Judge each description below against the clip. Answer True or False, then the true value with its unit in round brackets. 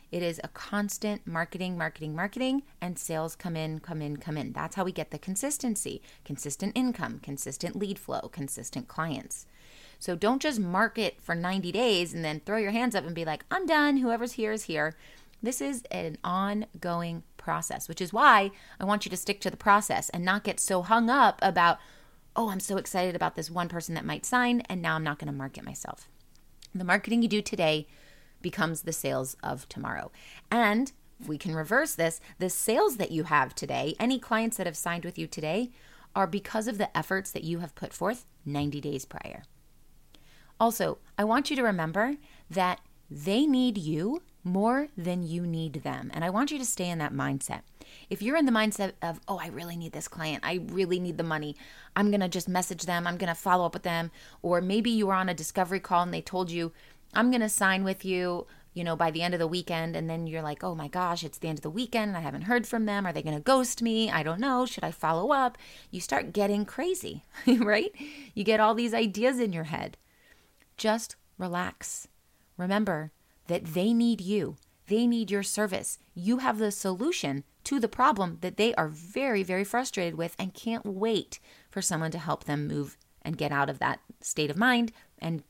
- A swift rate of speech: True (210 wpm)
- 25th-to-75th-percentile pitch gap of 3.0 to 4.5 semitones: False (5.1 semitones)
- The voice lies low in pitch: False (185 Hz)